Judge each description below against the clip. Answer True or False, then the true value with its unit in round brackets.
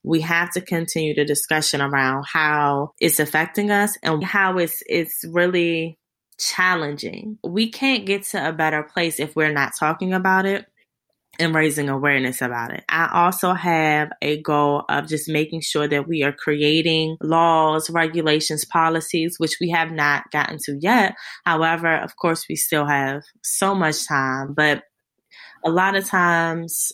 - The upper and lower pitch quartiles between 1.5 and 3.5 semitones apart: True (2.7 semitones)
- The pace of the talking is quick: False (160 wpm)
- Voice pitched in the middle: True (160 Hz)